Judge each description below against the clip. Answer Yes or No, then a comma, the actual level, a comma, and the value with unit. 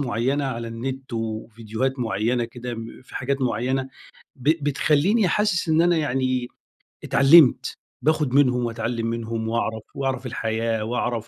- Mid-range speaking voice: No, low, 125 Hz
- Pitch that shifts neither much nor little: Yes, average, 3.1 semitones